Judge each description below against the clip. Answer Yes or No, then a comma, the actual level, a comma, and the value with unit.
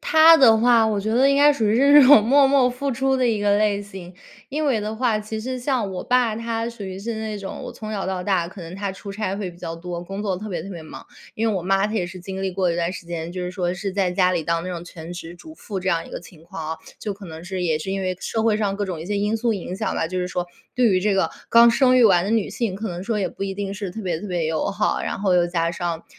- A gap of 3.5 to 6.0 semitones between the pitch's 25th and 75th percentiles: Yes, average, 3.9 semitones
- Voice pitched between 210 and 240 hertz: No, high, 195 Hz